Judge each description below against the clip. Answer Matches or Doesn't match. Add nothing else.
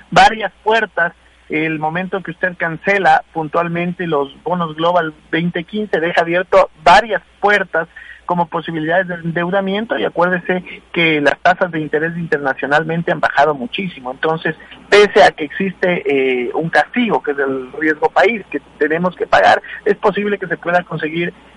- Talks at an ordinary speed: Matches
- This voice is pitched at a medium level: Matches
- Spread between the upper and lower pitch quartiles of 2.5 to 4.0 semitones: Matches